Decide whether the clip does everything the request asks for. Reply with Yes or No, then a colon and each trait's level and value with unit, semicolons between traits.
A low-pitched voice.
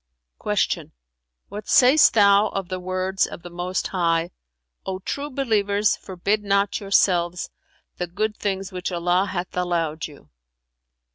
No: medium, 185 Hz